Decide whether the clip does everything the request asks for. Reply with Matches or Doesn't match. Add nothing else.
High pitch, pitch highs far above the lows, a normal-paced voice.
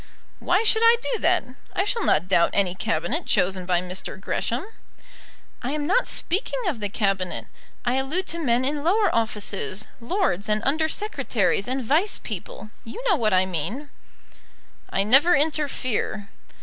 Matches